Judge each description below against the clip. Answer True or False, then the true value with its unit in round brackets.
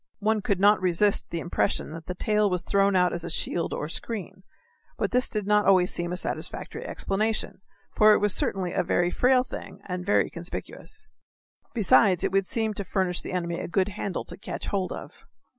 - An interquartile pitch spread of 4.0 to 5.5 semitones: False (2.7 semitones)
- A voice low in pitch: False (195 Hz)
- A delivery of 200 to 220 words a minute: True (205 wpm)